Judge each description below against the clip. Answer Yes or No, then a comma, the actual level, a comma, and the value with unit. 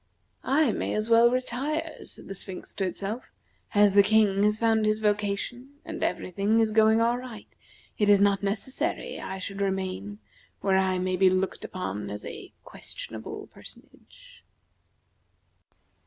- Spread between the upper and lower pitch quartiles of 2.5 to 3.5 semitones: Yes, average, 2.9 semitones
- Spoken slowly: No, average, 155 wpm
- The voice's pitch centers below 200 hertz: No, high, 205 Hz